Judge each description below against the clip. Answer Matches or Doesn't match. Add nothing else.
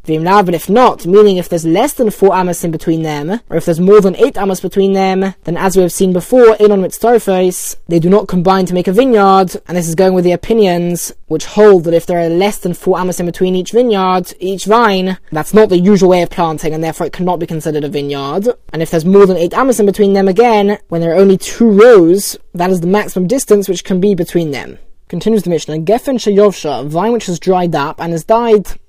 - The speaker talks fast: Matches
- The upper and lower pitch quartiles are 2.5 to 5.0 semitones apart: Matches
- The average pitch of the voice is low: Doesn't match